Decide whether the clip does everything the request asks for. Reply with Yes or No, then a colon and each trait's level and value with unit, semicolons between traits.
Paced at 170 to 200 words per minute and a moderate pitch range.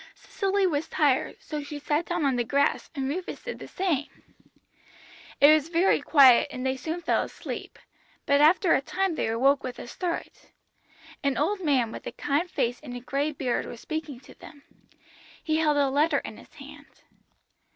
Yes: average, 185 wpm; average, 3.5 semitones